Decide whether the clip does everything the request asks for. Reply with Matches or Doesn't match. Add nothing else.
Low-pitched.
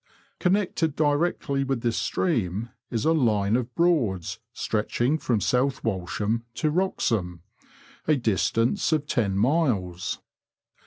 Matches